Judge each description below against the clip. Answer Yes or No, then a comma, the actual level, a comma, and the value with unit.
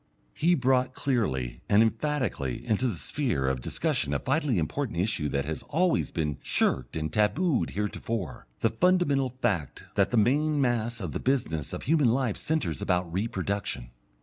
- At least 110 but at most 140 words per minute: No, average, 160 wpm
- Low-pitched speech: Yes, low, 110 Hz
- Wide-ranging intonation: Yes, wide, 8.9 semitones